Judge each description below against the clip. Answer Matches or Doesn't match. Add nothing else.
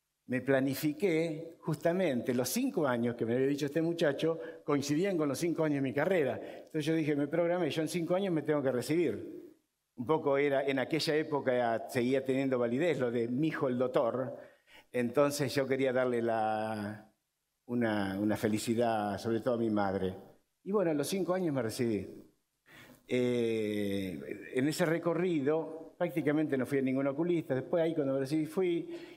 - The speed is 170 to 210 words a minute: Matches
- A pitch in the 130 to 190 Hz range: Matches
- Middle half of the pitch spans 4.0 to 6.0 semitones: Matches